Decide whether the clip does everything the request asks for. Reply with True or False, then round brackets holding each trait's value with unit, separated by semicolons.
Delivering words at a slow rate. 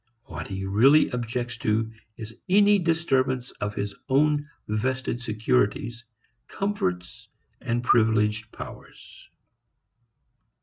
True (95 wpm)